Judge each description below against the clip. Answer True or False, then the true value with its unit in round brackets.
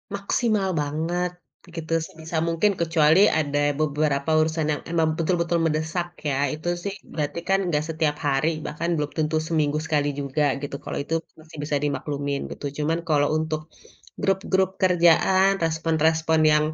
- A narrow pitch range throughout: True (2.2 semitones)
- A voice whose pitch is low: False (160 Hz)